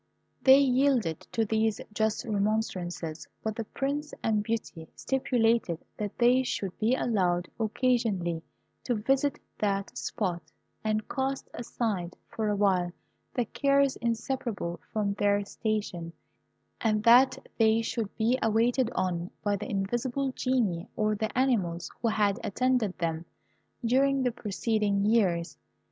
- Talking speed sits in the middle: No, slow, 130 wpm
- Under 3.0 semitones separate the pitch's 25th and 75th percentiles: No, average, 3.8 semitones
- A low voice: No, high, 220 Hz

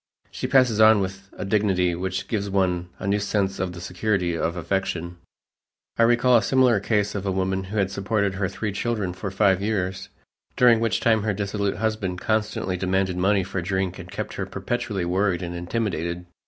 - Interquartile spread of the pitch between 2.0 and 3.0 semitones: Yes, narrow, 2.6 semitones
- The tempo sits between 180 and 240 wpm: Yes, average, 190 wpm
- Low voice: Yes, very low, 95 Hz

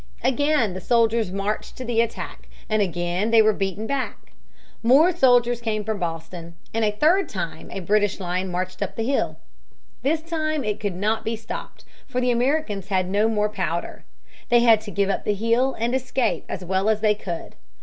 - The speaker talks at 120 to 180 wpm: No, average, 190 wpm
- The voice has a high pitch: Yes, high, 215 Hz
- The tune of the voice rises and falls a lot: No, average, 4.0 semitones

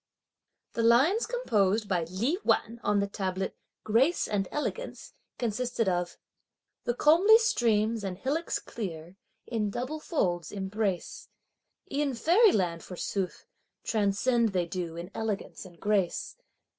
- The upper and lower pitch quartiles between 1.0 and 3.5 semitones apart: No, average, 5.2 semitones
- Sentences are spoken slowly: Yes, slow, 120 wpm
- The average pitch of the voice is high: Yes, high, 215 Hz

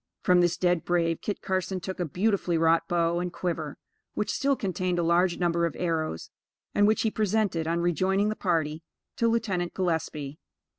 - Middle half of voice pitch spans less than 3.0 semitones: Yes, narrow, 2.4 semitones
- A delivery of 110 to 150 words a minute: No, average, 180 wpm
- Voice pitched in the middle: Yes, medium, 175 Hz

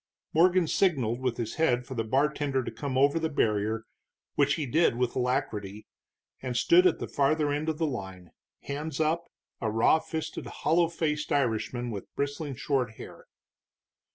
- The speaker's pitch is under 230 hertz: Yes, medium, 140 Hz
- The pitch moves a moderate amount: Yes, average, 5.0 semitones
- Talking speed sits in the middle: Yes, average, 165 wpm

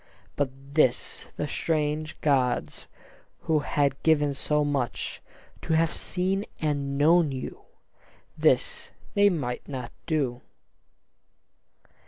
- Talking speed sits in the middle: No, slow, 105 wpm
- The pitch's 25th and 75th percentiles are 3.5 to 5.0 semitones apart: No, narrow, 2.5 semitones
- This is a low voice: No, medium, 150 Hz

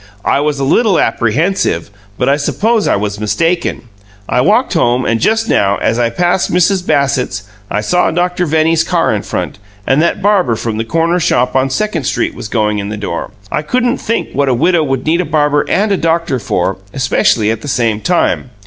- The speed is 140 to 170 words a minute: No, fast, 205 wpm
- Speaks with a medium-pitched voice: Yes, medium, 145 Hz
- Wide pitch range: Yes, wide, 7.4 semitones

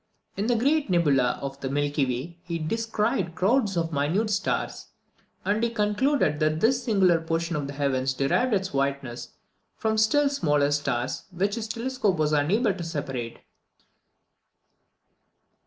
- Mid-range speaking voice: Yes, medium, 170 Hz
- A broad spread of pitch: Yes, wide, 7.2 semitones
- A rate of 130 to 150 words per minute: Yes, average, 145 wpm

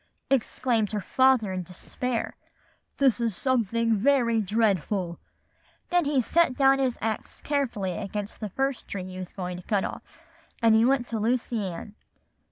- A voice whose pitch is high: Yes, high, 225 Hz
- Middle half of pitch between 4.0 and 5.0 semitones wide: Yes, average, 4.4 semitones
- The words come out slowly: No, average, 160 wpm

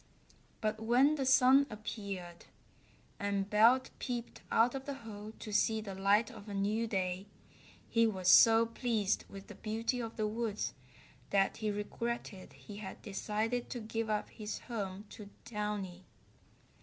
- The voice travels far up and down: No, narrow, 2.4 semitones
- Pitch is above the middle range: Yes, high, 215 Hz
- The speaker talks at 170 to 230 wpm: No, average, 155 wpm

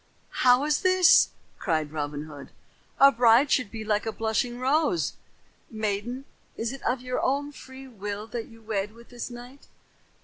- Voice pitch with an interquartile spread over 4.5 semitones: No, average, 3.8 semitones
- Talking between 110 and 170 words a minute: Yes, average, 165 wpm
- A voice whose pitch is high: Yes, high, 235 Hz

